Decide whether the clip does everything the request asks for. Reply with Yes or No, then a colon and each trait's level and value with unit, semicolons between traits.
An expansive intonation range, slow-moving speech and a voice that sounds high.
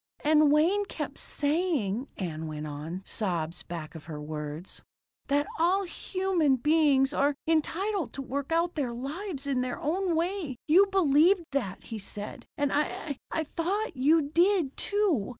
No: wide, 7.0 semitones; average, 150 wpm; very high, 290 Hz